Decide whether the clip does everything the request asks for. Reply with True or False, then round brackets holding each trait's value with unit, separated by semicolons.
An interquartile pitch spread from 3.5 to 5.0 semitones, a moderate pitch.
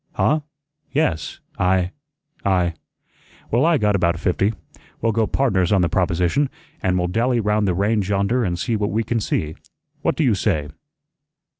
False (4.2 semitones; 100 Hz)